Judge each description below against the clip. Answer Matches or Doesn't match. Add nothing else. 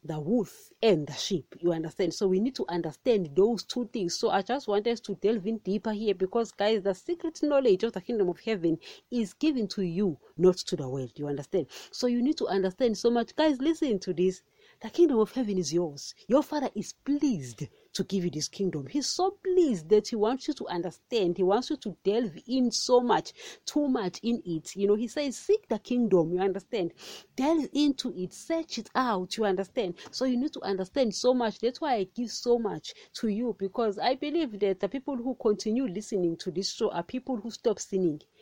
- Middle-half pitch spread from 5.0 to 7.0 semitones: Matches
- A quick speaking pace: Matches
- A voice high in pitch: Matches